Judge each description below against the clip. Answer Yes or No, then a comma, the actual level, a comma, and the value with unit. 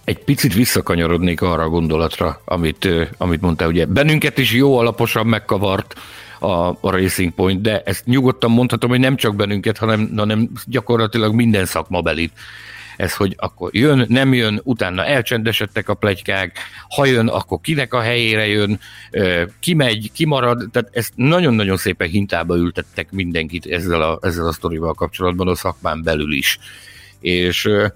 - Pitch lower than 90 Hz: No, low, 105 Hz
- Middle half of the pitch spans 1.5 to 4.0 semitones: No, average, 5.0 semitones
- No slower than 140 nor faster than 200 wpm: Yes, average, 150 wpm